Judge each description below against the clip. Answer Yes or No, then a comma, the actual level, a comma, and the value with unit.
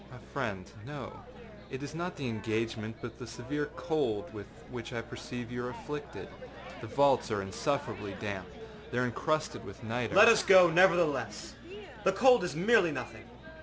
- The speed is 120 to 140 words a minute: No, average, 170 wpm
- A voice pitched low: Yes, low, 125 Hz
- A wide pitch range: Yes, wide, 5.7 semitones